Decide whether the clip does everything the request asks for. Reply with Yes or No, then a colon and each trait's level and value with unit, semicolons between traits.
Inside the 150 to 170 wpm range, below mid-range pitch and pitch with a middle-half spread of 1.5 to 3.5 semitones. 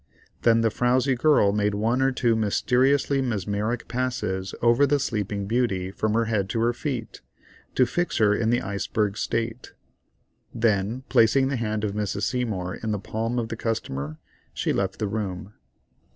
Yes: average, 165 wpm; low, 115 Hz; average, 3.1 semitones